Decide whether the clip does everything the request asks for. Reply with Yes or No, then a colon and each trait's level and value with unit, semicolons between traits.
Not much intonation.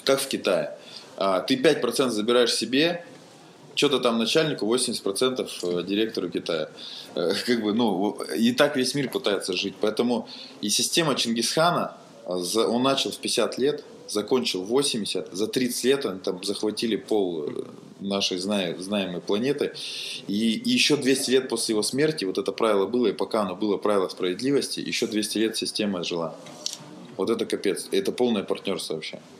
No: average, 4.8 semitones